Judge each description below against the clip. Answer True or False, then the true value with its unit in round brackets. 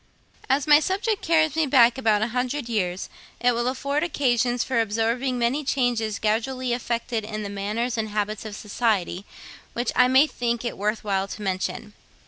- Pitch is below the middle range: False (235 Hz)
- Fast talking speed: False (175 wpm)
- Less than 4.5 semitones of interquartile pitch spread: True (3.5 semitones)